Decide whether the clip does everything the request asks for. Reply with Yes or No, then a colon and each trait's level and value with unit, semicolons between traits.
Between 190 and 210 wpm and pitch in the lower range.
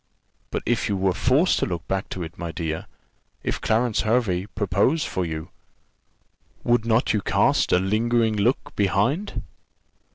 No: average, 155 wpm; low, 105 Hz